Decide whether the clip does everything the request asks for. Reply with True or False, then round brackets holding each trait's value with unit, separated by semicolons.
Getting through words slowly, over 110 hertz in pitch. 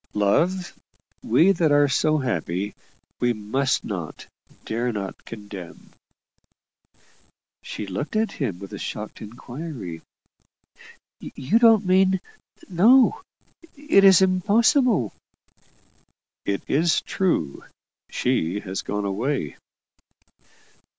True (95 wpm; 135 Hz)